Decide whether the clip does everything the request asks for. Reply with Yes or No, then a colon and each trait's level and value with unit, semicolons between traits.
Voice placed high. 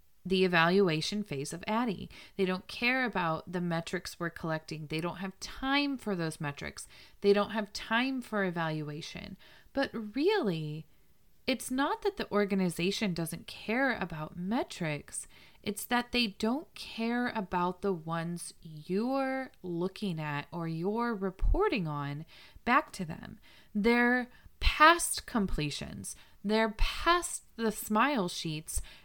Yes: high, 195 Hz